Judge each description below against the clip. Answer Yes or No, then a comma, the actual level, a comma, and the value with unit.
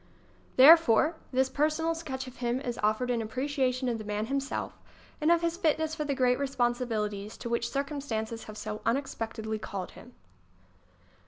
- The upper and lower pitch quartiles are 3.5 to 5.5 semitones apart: Yes, average, 4.1 semitones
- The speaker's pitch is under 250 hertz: No, very high, 255 Hz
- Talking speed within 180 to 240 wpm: No, average, 170 wpm